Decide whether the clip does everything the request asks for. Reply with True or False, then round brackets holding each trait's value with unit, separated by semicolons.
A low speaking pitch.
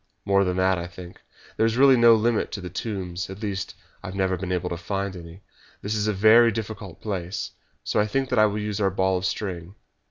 True (100 Hz)